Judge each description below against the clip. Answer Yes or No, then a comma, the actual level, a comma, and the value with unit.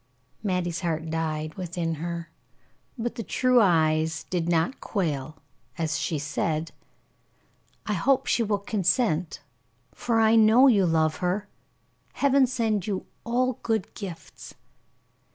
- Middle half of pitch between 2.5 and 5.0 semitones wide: No, wide, 5.6 semitones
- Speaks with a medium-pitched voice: Yes, medium, 180 Hz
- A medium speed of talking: No, slow, 125 wpm